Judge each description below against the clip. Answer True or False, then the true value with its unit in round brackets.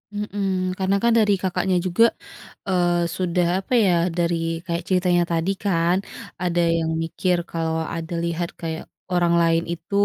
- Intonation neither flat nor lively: False (1.9 semitones)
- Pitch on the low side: False (175 Hz)